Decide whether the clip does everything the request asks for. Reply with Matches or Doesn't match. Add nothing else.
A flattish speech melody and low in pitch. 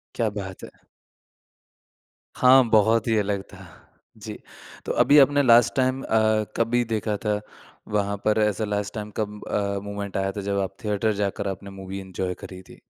Matches